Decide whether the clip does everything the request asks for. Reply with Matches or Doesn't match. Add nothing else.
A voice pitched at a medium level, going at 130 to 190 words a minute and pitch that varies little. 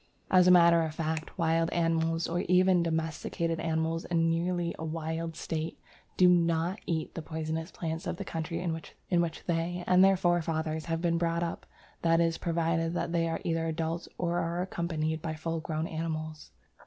Matches